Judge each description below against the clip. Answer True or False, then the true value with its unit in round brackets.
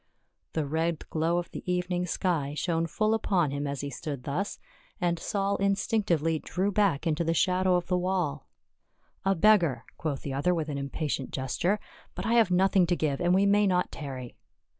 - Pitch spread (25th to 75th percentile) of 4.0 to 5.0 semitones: True (4.3 semitones)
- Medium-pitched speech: True (175 Hz)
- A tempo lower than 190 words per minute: False (205 wpm)